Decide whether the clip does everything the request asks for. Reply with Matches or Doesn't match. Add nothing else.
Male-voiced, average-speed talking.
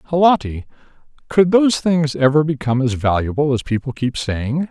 Matches